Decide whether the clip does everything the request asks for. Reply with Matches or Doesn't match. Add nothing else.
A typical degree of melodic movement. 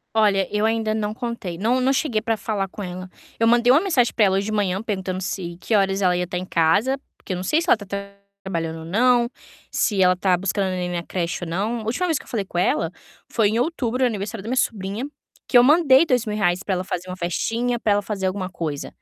Matches